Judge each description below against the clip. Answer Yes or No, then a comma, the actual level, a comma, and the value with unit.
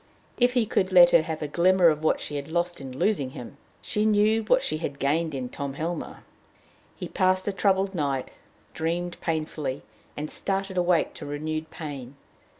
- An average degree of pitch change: Yes, average, 4.4 semitones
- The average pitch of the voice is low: No, medium, 165 Hz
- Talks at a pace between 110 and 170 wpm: No, average, 185 wpm